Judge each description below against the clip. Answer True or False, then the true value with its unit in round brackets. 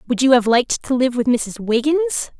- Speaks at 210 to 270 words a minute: True (225 wpm)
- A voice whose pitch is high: True (255 Hz)